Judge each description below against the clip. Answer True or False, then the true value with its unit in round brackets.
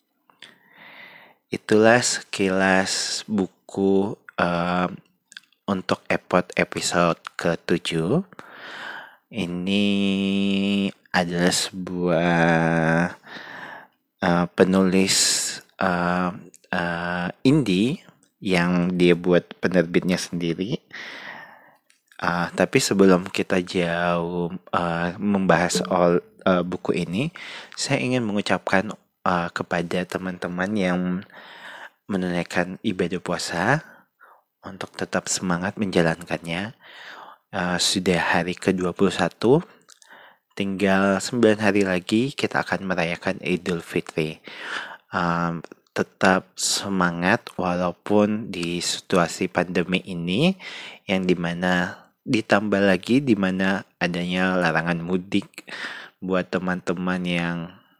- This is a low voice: True (90 Hz)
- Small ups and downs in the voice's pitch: True (2.0 semitones)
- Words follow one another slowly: True (80 wpm)